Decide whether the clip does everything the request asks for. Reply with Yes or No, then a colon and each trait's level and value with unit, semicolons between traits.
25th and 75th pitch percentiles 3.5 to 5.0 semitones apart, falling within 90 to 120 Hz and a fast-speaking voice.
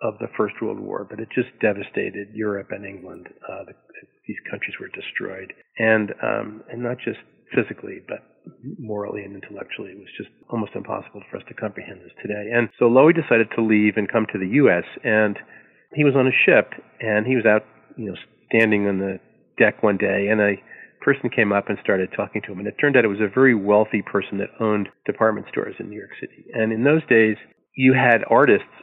No: narrow, 2.4 semitones; low, 110 Hz; fast, 215 wpm